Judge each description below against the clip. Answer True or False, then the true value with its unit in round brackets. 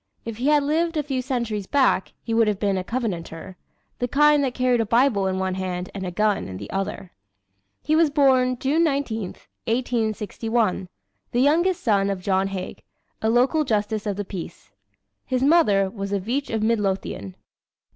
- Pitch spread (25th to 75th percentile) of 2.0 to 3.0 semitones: False (5.3 semitones)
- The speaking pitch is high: True (225 Hz)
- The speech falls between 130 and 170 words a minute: False (180 wpm)